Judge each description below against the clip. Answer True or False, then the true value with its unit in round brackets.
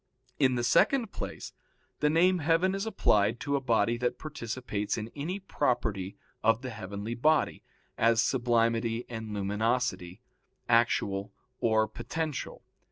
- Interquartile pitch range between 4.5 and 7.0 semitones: True (5.0 semitones)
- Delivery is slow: True (130 wpm)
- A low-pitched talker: True (120 Hz)